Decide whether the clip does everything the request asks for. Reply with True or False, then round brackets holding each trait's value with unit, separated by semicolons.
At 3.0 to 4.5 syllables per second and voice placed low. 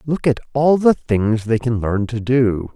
True (4.1 syllables/s; 120 Hz)